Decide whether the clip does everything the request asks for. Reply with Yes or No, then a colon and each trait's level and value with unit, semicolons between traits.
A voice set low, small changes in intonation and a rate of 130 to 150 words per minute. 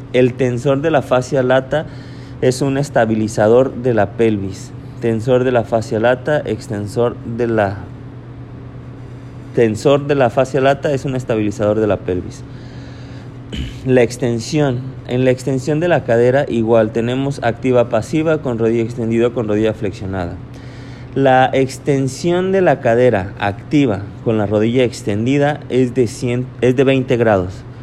Yes: low, 125 Hz; narrow, 2.3 semitones; average, 140 wpm